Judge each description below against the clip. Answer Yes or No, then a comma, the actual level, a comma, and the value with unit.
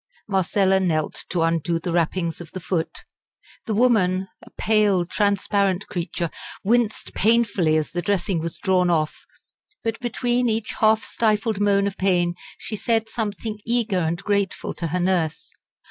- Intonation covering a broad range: No, average, 3.8 semitones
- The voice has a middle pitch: No, high, 195 Hz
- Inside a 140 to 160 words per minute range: Yes, average, 150 wpm